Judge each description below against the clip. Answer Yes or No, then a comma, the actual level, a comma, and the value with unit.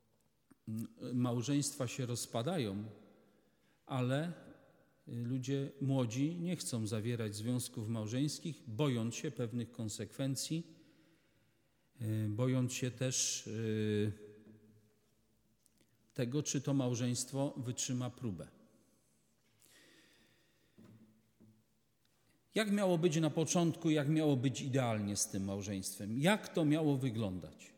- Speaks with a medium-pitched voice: No, low, 125 Hz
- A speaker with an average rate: No, slow, 85 wpm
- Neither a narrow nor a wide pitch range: Yes, average, 4.3 semitones